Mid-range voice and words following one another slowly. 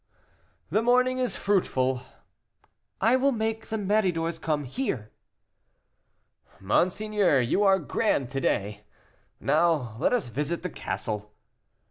Yes: medium, 170 Hz; slow, 115 wpm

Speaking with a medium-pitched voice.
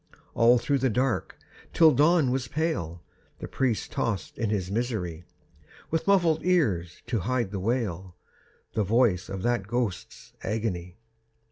No: low, 115 Hz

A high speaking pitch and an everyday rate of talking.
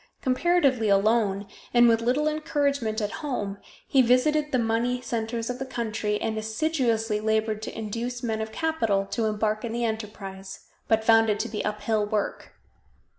Yes: high, 225 Hz; average, 165 wpm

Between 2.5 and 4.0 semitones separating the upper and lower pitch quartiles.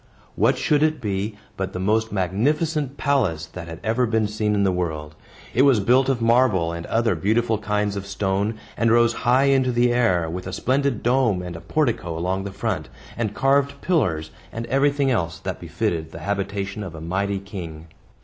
No: average, 5.1 semitones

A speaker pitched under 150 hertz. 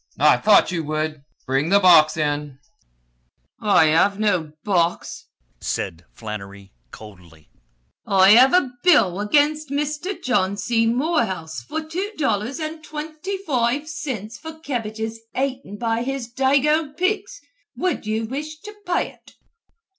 No: high, 230 Hz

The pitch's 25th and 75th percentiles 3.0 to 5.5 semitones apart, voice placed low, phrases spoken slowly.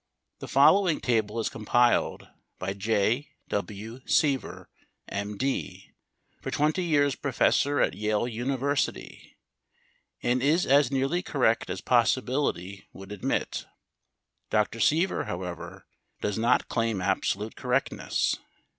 Yes: average, 5.1 semitones; low, 120 Hz; slow, 110 wpm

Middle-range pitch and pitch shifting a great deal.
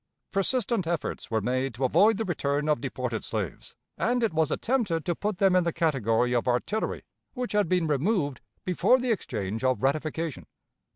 Yes: medium, 160 Hz; wide, 7.9 semitones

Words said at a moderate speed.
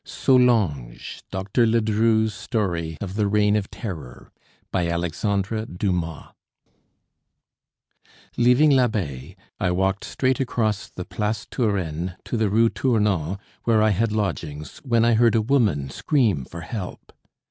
No: slow, 125 wpm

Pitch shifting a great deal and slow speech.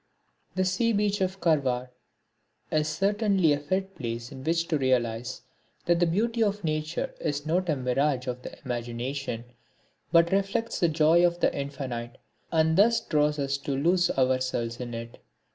No: wide, 6.0 semitones; average, 160 wpm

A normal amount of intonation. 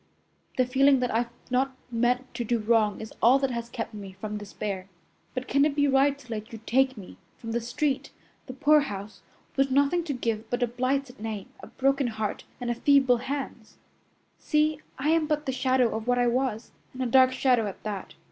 Yes: average, 3.3 semitones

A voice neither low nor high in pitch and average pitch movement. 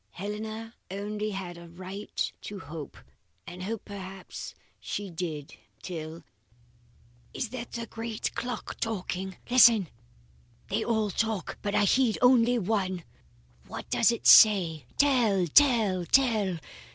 No: high, 205 Hz; average, 3.7 semitones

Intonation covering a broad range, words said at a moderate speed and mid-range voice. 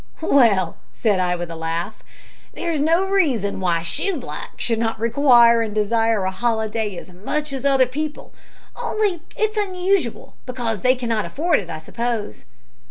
No: wide, 6.6 semitones; average, 160 wpm; high, 230 Hz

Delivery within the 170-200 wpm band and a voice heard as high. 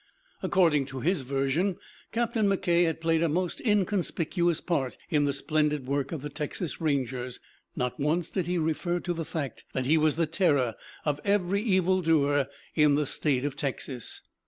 No: average, 175 wpm; medium, 155 Hz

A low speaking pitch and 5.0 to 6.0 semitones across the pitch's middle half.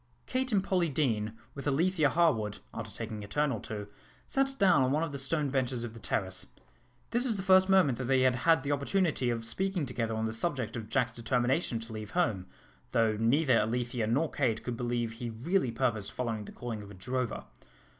Yes: low, 125 Hz; wide, 5.5 semitones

